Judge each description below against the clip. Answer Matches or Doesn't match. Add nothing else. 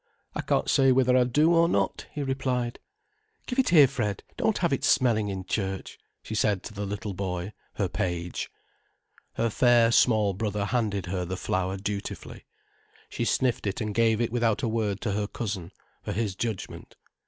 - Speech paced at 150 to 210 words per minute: Matches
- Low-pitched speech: Matches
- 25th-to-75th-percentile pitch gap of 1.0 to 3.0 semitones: Doesn't match